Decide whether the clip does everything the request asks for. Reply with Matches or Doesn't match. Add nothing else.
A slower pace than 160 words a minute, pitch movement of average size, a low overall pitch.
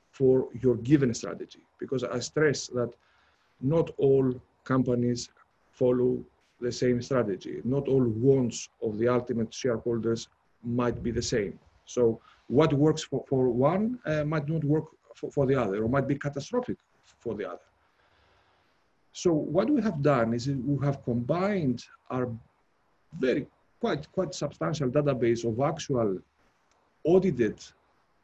Matches